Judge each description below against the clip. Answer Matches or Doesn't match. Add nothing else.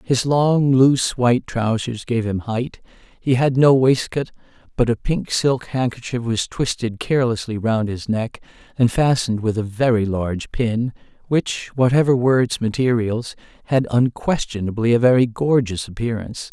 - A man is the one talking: Matches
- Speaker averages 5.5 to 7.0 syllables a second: Doesn't match